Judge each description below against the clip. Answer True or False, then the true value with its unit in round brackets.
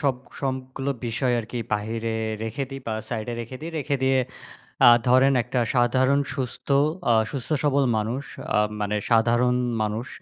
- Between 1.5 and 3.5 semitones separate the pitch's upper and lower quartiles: True (2.8 semitones)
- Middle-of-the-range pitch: False (125 Hz)